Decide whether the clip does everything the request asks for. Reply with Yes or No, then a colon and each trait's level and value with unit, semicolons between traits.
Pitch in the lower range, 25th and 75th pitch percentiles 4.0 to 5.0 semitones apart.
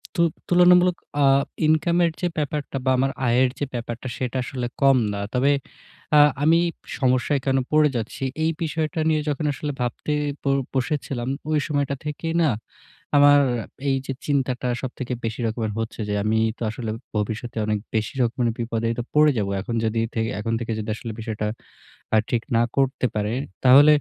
Yes: low, 130 Hz; average, 4.5 semitones